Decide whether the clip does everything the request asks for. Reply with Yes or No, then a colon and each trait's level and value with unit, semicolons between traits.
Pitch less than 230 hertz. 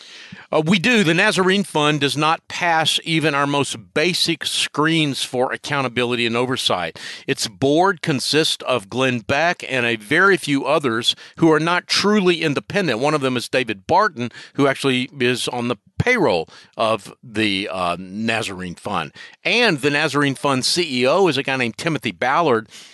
Yes: medium, 140 Hz